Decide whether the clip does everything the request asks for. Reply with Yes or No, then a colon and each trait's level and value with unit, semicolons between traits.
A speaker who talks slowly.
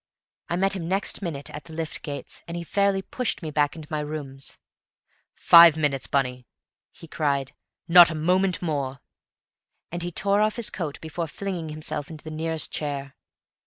No: average, 175 wpm